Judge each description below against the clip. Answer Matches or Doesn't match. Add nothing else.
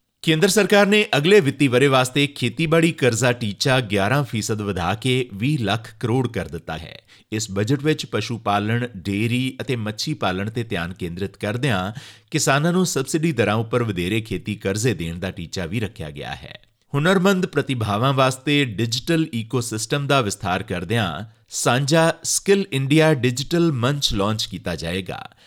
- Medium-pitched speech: Doesn't match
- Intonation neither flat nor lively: Doesn't match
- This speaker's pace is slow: Doesn't match